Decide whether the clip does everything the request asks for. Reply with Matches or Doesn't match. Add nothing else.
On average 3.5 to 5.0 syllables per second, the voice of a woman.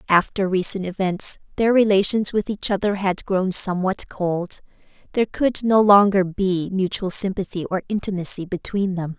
Matches